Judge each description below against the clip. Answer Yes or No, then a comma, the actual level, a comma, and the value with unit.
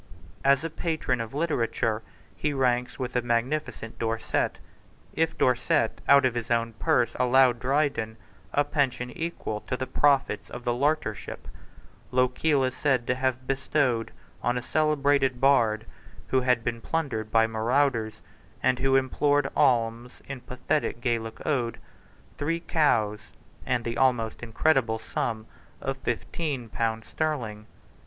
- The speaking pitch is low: Yes, low, 125 Hz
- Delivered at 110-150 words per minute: Yes, average, 140 wpm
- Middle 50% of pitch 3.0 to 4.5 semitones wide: Yes, average, 3.4 semitones